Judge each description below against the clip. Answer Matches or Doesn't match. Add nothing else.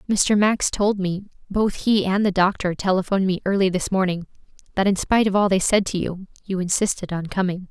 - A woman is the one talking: Matches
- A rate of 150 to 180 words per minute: Doesn't match